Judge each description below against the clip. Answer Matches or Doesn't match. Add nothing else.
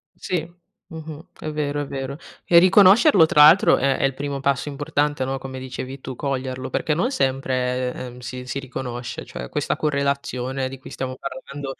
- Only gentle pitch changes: Matches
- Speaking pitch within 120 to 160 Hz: Matches